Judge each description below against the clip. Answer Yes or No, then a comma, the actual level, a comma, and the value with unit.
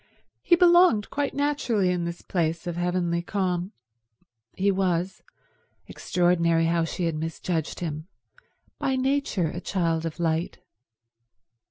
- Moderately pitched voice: Yes, medium, 175 Hz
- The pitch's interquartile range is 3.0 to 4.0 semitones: Yes, average, 3.3 semitones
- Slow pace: Yes, slow, 115 wpm